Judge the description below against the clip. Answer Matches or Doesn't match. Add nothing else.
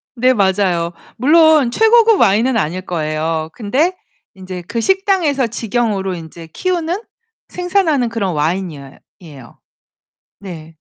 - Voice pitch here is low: Doesn't match